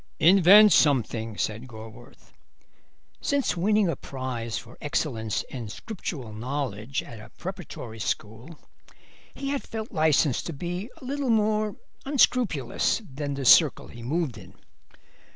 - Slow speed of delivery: Yes, slow, 130 wpm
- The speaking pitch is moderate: Yes, medium, 145 Hz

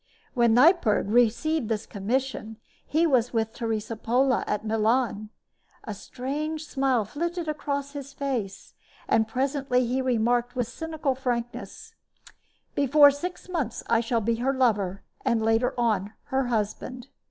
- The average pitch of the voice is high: Yes, high, 245 Hz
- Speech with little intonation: No, average, 3.8 semitones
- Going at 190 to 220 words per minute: No, slow, 135 wpm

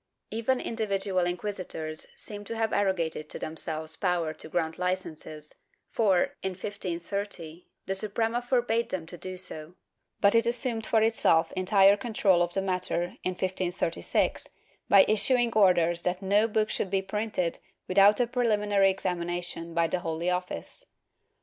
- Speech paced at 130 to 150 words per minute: Yes, average, 145 wpm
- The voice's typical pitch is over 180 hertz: Yes, high, 190 Hz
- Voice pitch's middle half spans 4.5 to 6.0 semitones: No, average, 3.4 semitones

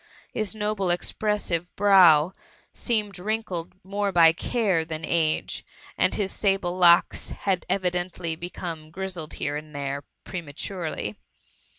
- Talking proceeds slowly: Yes, slow, 130 wpm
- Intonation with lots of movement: No, average, 3.4 semitones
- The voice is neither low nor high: Yes, medium, 180 Hz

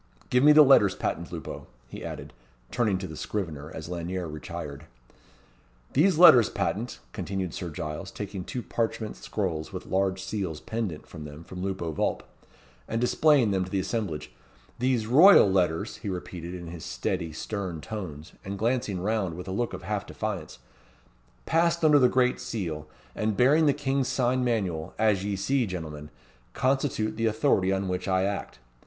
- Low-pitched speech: Yes, low, 100 Hz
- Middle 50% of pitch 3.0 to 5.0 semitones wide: No, wide, 5.4 semitones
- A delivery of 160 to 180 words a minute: Yes, average, 170 wpm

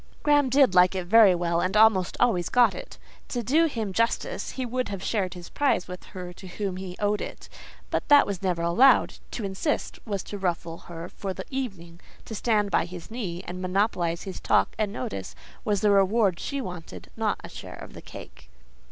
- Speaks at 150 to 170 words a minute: No, average, 200 wpm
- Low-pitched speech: No, high, 195 Hz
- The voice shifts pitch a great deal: No, average, 4.2 semitones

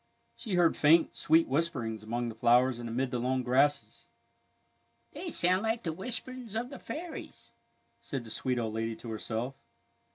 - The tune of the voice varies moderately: No, wide, 7.6 semitones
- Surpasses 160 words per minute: Yes, average, 170 wpm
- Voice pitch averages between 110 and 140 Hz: Yes, low, 135 Hz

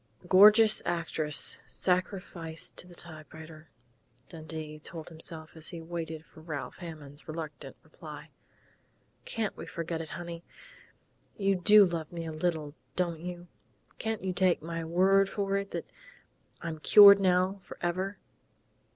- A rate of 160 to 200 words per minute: No, slow, 135 wpm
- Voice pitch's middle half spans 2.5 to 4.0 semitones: Yes, average, 2.8 semitones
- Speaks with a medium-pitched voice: Yes, medium, 170 Hz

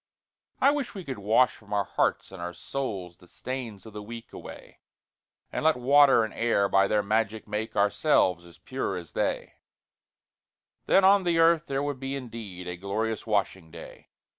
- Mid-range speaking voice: No, low, 110 Hz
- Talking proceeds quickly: No, average, 180 wpm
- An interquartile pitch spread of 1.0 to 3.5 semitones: No, wide, 5.6 semitones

